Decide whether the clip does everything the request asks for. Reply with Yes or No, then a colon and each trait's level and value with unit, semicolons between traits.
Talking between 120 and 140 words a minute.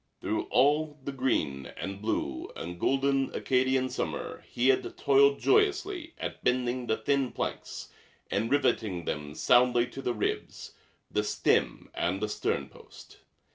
Yes: slow, 135 wpm